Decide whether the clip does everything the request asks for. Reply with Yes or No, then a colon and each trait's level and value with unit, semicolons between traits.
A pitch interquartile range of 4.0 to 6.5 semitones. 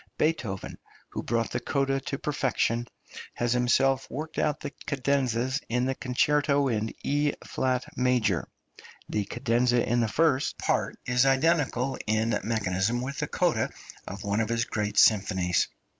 No: average, 3.4 semitones